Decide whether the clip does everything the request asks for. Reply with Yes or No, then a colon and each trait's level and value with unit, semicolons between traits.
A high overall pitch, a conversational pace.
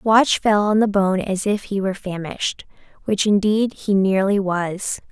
Yes: high, 200 Hz; average, 175 wpm